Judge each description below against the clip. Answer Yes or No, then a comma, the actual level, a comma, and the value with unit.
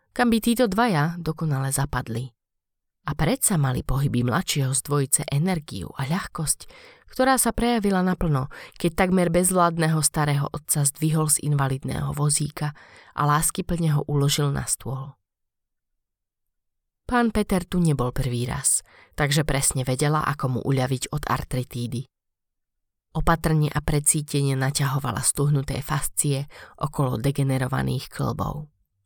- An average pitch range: Yes, average, 3.5 semitones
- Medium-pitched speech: Yes, medium, 145 Hz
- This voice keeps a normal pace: Yes, average, 120 wpm